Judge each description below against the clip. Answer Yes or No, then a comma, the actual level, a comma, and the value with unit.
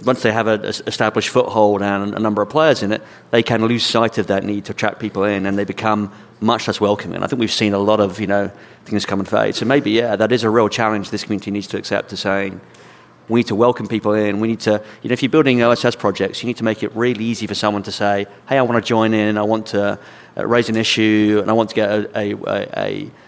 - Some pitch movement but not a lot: No, narrow, 1.9 semitones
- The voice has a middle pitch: No, low, 110 Hz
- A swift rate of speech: Yes, fast, 275 wpm